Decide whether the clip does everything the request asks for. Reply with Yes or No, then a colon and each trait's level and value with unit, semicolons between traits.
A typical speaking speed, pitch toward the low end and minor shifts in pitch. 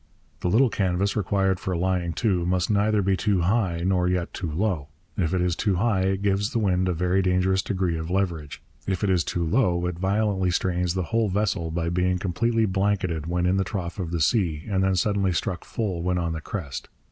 No: fast, 215 wpm; very low, 95 Hz; narrow, 2.3 semitones